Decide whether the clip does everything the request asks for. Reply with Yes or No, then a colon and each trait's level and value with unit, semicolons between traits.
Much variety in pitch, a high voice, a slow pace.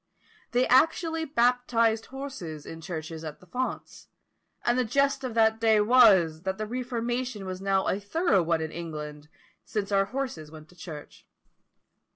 No: wide, 7.0 semitones; high, 210 Hz; average, 160 wpm